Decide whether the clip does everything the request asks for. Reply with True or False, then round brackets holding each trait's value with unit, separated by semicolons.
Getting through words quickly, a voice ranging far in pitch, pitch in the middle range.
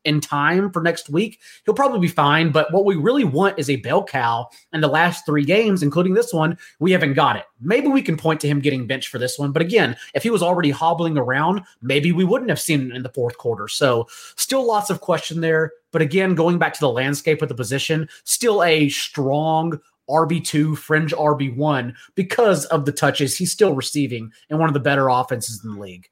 False (225 wpm; 3.8 semitones; 160 Hz)